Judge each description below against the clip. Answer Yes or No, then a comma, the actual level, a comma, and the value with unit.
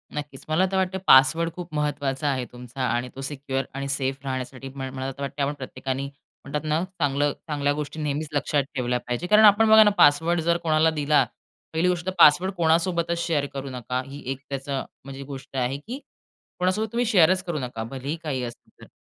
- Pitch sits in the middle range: Yes, medium, 145 Hz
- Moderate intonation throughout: Yes, average, 3.8 semitones